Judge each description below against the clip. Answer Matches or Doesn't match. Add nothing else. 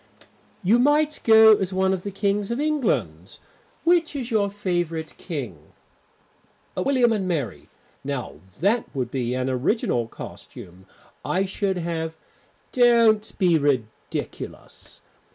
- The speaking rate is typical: Doesn't match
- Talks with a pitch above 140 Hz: Matches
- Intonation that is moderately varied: Doesn't match